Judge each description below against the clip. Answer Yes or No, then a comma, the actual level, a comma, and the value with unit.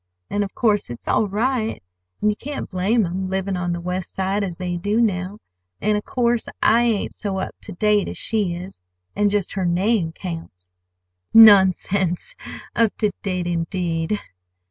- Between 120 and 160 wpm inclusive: No, average, 170 wpm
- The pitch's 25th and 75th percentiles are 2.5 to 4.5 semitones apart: Yes, average, 2.9 semitones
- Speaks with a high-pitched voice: Yes, high, 195 Hz